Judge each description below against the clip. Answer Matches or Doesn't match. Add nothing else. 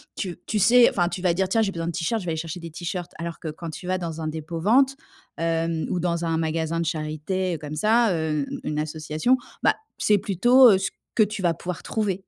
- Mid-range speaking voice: Matches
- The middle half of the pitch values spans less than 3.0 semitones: Doesn't match